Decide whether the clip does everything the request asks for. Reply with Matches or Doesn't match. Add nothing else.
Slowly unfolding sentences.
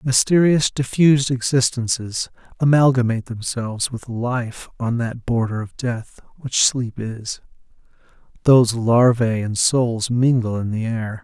Matches